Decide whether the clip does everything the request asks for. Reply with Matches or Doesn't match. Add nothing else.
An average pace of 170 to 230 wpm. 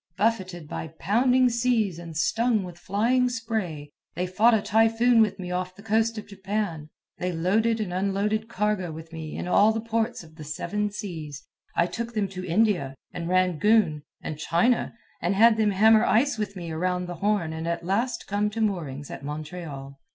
Matches